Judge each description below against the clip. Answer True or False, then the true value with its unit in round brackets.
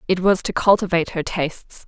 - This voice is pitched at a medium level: True (180 Hz)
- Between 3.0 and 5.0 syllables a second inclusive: False (5.9 syllables/s)